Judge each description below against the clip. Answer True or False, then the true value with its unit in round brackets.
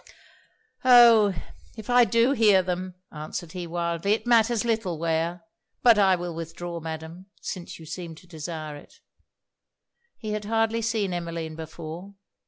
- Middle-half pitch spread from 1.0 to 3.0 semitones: False (4.8 semitones)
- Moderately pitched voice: True (180 Hz)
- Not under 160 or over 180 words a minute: False (145 wpm)